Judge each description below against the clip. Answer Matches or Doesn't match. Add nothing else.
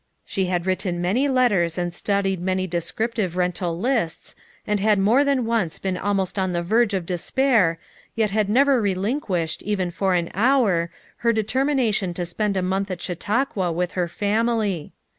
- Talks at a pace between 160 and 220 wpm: Matches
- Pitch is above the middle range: Matches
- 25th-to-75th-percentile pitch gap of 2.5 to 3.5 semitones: Doesn't match